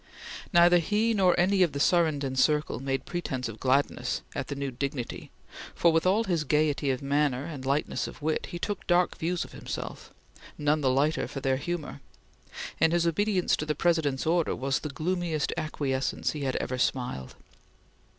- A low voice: No, medium, 150 Hz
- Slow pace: No, average, 180 wpm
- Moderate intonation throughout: Yes, average, 4.1 semitones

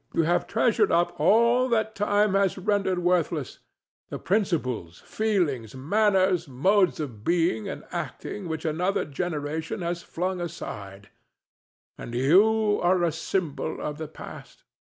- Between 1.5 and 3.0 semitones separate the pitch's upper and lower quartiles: No, average, 5.0 semitones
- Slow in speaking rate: Yes, slow, 125 wpm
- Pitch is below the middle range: No, medium, 175 Hz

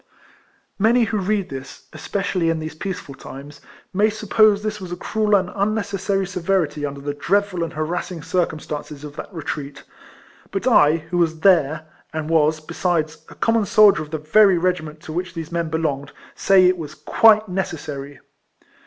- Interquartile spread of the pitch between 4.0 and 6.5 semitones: Yes, average, 4.5 semitones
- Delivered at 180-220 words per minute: No, average, 170 wpm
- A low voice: No, medium, 175 Hz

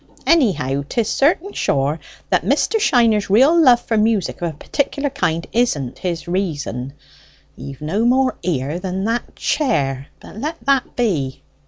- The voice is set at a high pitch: Yes, high, 205 Hz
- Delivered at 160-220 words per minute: No, average, 150 wpm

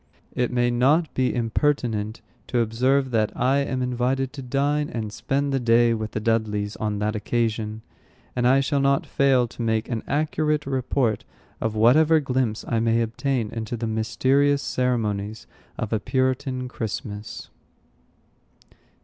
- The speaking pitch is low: Yes, low, 120 Hz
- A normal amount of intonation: Yes, average, 3.4 semitones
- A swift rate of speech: No, average, 150 wpm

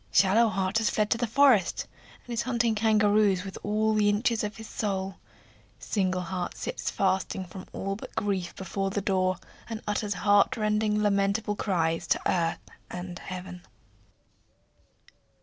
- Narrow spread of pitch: Yes, narrow, 2.3 semitones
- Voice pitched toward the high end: Yes, high, 205 Hz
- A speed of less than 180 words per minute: Yes, average, 150 wpm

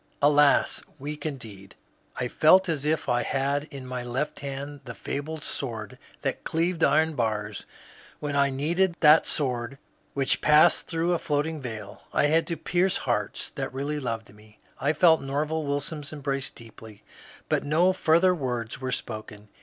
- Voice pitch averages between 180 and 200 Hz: No, medium, 145 Hz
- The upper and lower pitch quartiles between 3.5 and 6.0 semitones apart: Yes, average, 4.1 semitones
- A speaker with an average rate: Yes, average, 160 wpm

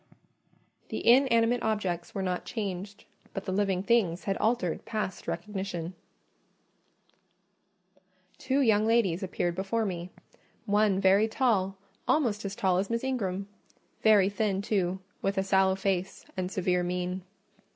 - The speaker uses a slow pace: Yes, slow, 130 wpm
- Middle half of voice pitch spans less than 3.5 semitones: Yes, average, 2.8 semitones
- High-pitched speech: Yes, high, 195 Hz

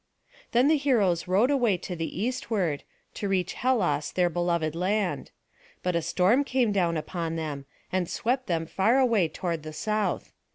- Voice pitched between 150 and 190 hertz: Yes, medium, 185 Hz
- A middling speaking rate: Yes, average, 165 wpm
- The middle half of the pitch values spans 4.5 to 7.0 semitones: Yes, wide, 5.5 semitones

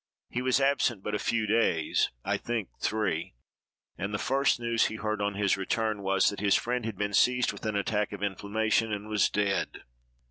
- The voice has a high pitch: No, low, 105 Hz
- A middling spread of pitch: No, narrow, 2.1 semitones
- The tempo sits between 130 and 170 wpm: No, average, 200 wpm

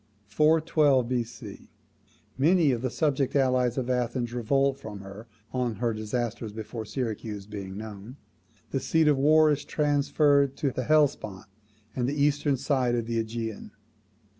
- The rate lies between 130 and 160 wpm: Yes, average, 140 wpm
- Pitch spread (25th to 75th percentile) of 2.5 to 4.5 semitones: Yes, average, 4.2 semitones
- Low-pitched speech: Yes, low, 125 Hz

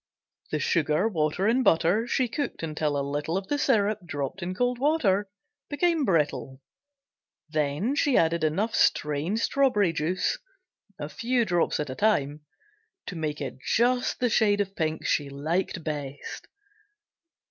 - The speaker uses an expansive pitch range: Yes, wide, 6.9 semitones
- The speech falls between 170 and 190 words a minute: No, average, 145 wpm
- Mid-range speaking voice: Yes, medium, 175 Hz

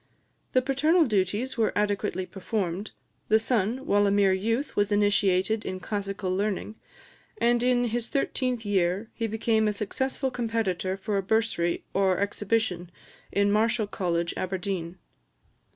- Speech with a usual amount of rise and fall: Yes, average, 3.1 semitones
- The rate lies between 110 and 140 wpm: Yes, slow, 135 wpm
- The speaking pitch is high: Yes, high, 205 Hz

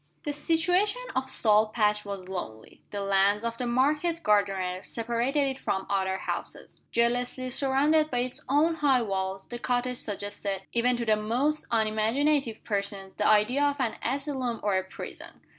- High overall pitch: Yes, high, 235 Hz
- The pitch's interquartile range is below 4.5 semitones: No, average, 5.0 semitones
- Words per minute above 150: Yes, average, 160 wpm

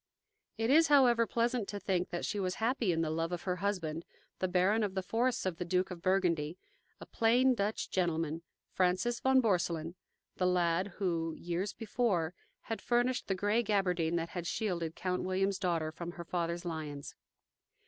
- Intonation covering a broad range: No, average, 4.2 semitones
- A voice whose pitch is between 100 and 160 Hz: No, medium, 185 Hz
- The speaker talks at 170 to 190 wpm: Yes, average, 180 wpm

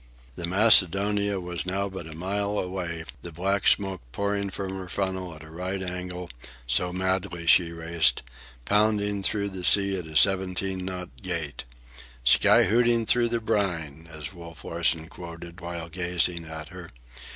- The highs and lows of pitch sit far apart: No, average, 2.8 semitones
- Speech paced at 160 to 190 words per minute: No, average, 150 wpm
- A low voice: Yes, very low, 90 Hz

